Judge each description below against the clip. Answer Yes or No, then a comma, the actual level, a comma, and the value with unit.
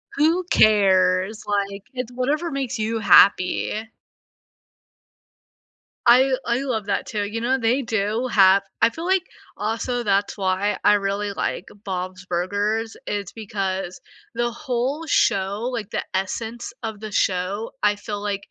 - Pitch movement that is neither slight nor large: Yes, average, 3.3 semitones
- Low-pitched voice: No, high, 215 Hz